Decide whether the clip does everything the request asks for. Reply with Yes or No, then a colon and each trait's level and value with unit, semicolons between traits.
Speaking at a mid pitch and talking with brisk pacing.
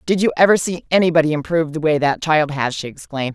Yes: medium, 160 Hz; fast, 235 wpm